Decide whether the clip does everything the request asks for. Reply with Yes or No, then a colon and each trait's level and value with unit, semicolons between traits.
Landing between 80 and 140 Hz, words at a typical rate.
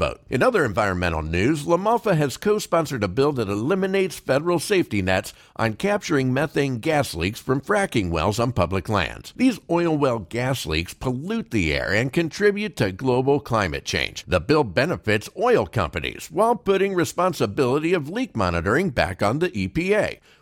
Yes: low, 135 Hz; average, 160 wpm